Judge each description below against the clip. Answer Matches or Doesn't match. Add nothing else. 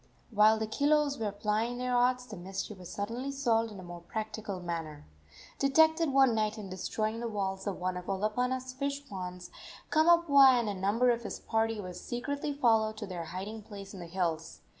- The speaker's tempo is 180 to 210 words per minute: Matches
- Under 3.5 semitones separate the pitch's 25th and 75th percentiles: Doesn't match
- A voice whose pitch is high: Matches